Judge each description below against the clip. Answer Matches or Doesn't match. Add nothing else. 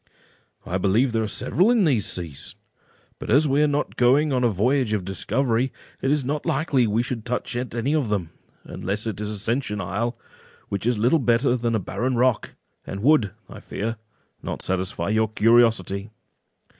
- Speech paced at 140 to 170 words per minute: Doesn't match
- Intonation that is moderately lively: Matches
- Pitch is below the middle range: Matches